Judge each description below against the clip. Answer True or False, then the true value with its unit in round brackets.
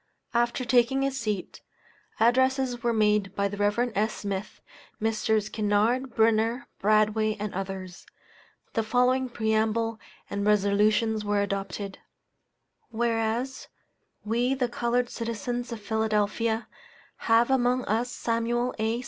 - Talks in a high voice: True (225 Hz)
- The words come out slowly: True (115 wpm)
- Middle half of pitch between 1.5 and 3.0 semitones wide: True (2.4 semitones)